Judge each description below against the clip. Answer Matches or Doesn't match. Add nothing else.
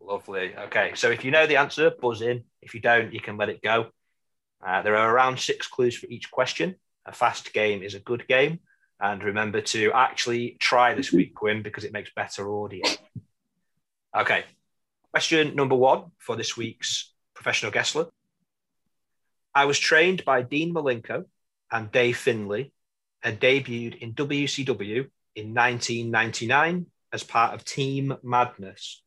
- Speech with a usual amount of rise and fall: Matches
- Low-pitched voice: Matches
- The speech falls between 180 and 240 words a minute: Doesn't match